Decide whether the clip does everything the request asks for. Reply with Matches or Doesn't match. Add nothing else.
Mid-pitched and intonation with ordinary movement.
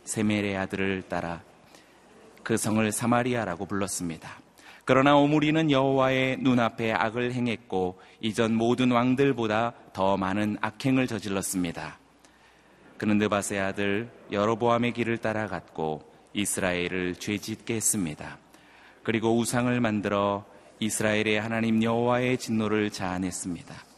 Doesn't match